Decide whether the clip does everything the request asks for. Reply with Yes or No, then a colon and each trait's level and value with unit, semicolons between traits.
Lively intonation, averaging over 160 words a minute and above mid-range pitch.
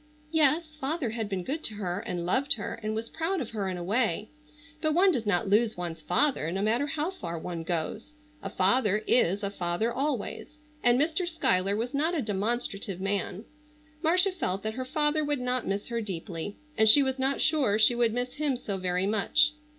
Yes: wide, 6.8 semitones; fast, 205 wpm; high, 225 Hz